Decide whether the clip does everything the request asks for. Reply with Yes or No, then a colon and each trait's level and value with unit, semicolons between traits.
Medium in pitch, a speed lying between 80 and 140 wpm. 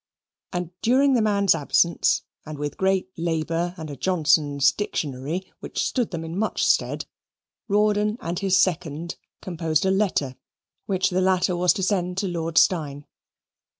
No: medium, 175 Hz; average, 150 wpm